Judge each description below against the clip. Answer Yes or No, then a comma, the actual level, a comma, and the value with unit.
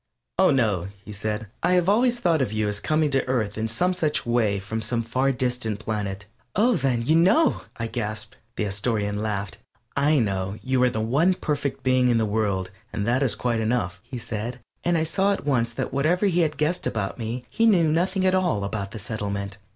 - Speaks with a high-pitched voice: No, low, 120 Hz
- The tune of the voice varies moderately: No, wide, 6.5 semitones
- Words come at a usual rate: No, fast, 215 wpm